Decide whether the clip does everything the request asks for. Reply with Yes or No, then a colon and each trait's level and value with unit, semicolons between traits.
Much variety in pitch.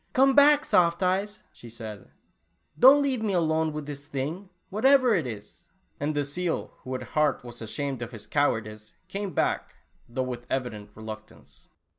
Yes: wide, 8.3 semitones